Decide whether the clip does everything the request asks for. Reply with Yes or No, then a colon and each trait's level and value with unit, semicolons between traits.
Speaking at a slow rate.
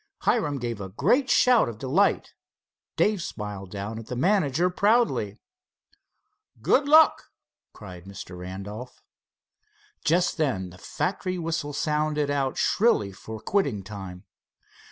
Yes: slow, 120 wpm